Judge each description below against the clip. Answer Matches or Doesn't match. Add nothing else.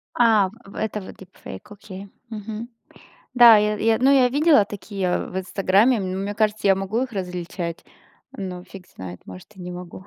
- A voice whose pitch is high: Matches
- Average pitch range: Matches